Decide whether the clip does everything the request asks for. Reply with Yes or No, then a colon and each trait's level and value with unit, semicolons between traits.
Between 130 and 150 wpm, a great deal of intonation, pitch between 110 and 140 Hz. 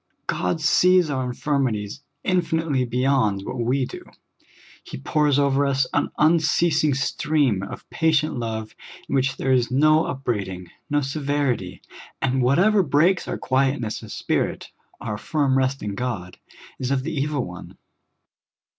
No: average, 140 wpm; average, 3.7 semitones; low, 135 Hz